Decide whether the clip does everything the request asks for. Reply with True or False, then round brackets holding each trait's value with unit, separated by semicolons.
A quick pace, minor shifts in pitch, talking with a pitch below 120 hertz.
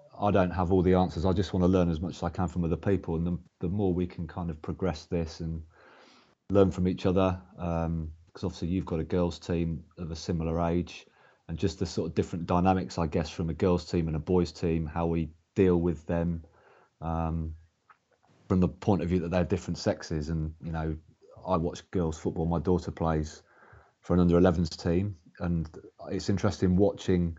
True (215 wpm; 2.0 semitones; 85 Hz)